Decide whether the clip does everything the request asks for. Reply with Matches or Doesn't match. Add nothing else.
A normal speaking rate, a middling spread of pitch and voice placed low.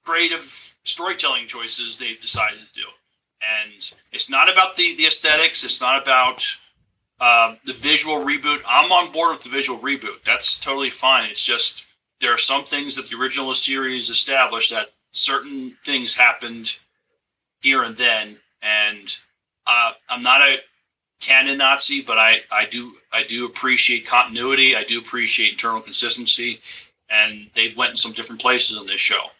Matches